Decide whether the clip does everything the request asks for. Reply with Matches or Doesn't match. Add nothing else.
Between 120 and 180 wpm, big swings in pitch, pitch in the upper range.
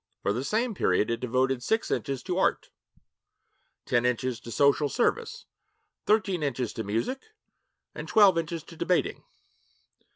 Doesn't match